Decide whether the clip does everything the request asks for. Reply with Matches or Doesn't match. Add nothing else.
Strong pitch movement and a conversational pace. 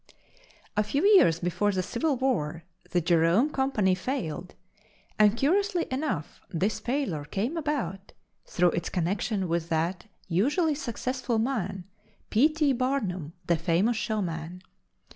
Doesn't match